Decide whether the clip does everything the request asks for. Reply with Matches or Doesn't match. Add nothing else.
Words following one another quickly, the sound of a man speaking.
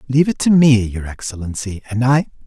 Doesn't match